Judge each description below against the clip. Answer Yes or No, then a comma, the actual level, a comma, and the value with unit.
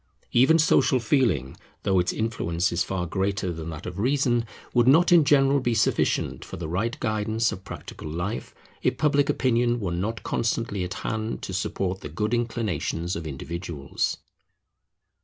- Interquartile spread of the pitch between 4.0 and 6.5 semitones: Yes, wide, 5.5 semitones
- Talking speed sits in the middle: Yes, average, 160 wpm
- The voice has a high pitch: No, low, 105 Hz